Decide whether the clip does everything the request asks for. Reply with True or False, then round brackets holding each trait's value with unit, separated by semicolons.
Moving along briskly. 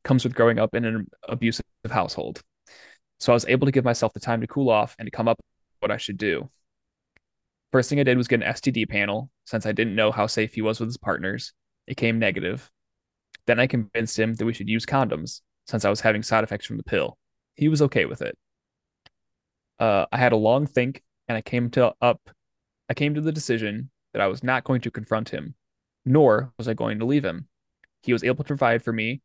True (230 wpm)